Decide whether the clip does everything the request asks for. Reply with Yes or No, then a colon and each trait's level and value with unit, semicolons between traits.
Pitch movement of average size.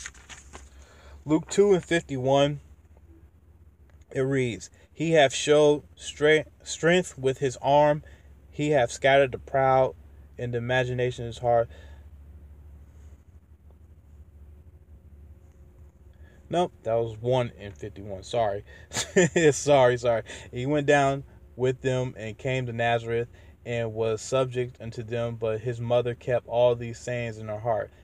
No: wide, 8.2 semitones